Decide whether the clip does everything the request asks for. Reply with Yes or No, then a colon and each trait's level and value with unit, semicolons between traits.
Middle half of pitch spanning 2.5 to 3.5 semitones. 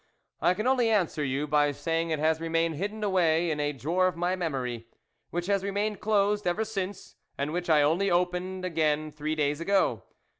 No: average, 4.2 semitones